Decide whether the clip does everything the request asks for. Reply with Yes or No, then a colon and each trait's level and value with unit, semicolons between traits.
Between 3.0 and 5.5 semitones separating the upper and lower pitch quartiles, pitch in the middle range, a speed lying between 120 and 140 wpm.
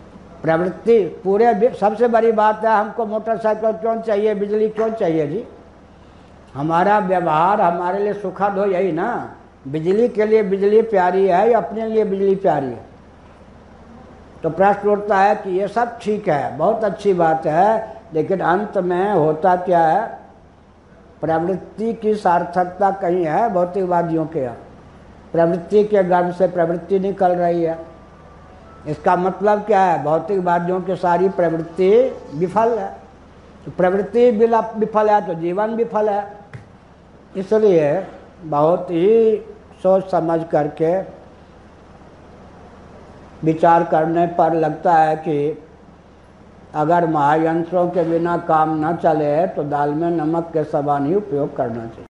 Yes: average, 5.1 semitones; medium, 175 Hz; average, 135 wpm